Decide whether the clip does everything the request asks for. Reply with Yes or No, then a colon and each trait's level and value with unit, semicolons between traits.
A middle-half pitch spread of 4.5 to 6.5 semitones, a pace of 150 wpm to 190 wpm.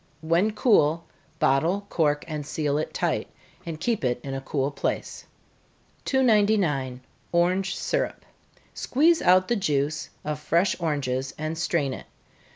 No: average, 5.2 semitones; slow, 135 wpm